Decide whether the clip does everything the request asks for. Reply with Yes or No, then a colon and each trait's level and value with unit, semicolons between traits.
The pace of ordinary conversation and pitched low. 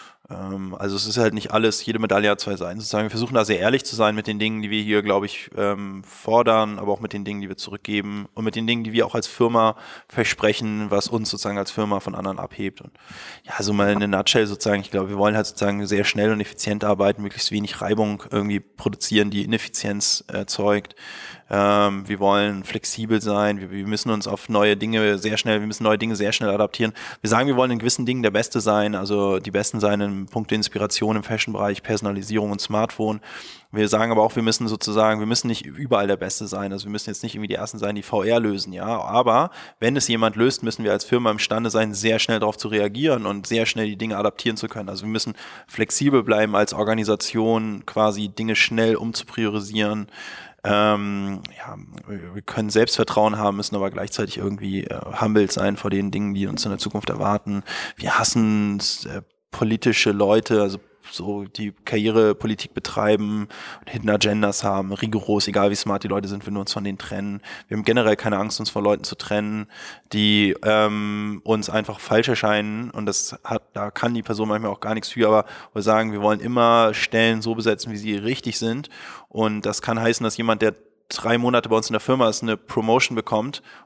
No: fast, 210 wpm; low, 105 Hz